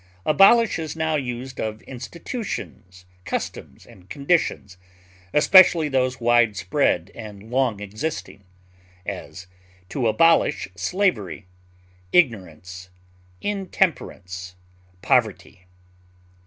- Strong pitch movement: Yes, wide, 8.4 semitones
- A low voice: Yes, low, 120 Hz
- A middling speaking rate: No, slow, 85 wpm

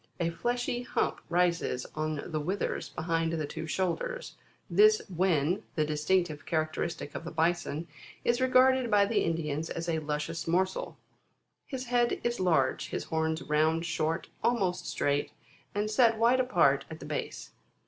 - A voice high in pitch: No, medium, 170 Hz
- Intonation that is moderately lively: No, wide, 6.3 semitones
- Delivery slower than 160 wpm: Yes, average, 150 wpm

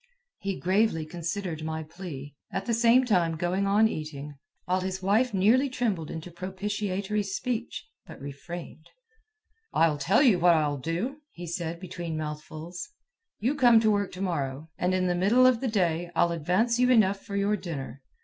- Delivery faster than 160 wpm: Yes, average, 170 wpm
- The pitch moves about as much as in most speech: Yes, average, 4.5 semitones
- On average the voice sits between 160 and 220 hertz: Yes, medium, 185 Hz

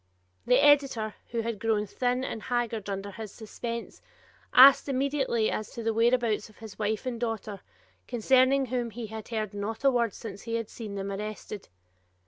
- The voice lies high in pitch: Yes, high, 225 Hz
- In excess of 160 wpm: Yes, average, 175 wpm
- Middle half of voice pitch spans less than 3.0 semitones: Yes, narrow, 2.5 semitones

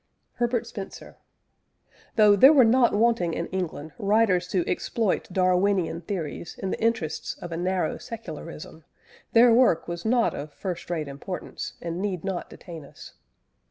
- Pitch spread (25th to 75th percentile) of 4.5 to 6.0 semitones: Yes, average, 4.9 semitones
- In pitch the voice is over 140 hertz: Yes, medium, 185 Hz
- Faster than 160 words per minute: No, average, 150 wpm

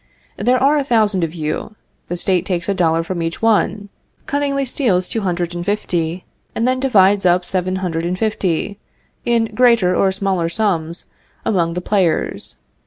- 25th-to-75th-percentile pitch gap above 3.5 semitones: Yes, average, 4.1 semitones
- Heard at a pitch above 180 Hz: Yes, high, 190 Hz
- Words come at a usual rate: Yes, average, 170 wpm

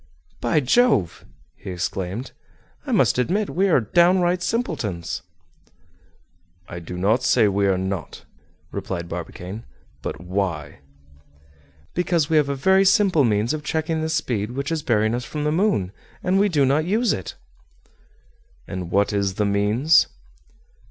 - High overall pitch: No, low, 125 Hz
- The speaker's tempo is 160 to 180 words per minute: No, average, 150 wpm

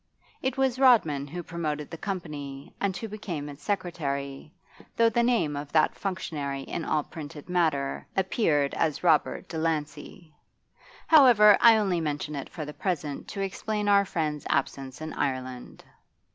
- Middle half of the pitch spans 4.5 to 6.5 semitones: Yes, wide, 5.4 semitones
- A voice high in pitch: No, medium, 160 Hz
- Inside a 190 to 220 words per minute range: No, average, 150 wpm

